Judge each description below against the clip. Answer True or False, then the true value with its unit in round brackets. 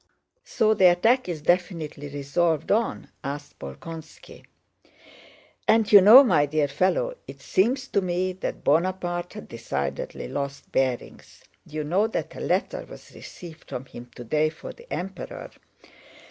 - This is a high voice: False (175 Hz)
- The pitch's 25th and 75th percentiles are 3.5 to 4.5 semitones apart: False (5.6 semitones)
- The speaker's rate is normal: True (145 wpm)